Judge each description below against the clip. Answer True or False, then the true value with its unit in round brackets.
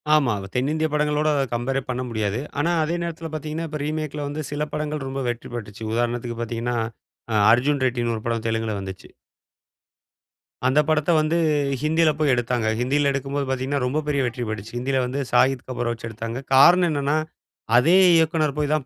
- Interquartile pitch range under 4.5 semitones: True (4.1 semitones)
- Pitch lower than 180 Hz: True (135 Hz)